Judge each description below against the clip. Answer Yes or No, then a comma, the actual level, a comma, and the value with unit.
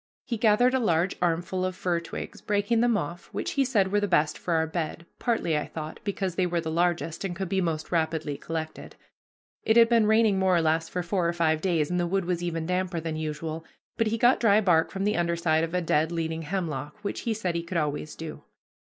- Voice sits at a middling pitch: Yes, medium, 175 Hz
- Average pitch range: Yes, average, 3.5 semitones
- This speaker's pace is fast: Yes, fast, 235 wpm